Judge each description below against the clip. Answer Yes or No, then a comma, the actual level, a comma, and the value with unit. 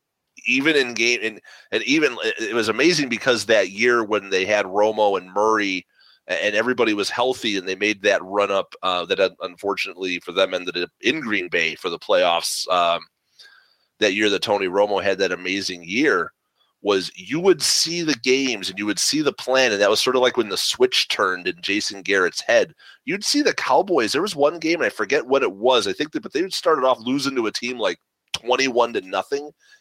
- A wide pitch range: Yes, wide, 8.7 semitones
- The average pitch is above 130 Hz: No, low, 125 Hz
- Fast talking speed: Yes, fast, 215 wpm